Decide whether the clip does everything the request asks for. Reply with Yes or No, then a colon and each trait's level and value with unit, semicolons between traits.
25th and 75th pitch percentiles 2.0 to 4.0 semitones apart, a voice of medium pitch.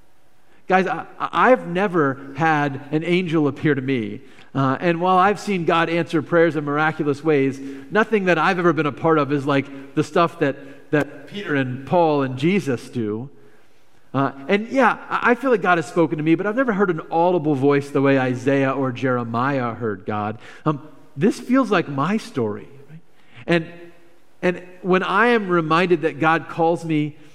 No: average, 4.4 semitones; medium, 155 Hz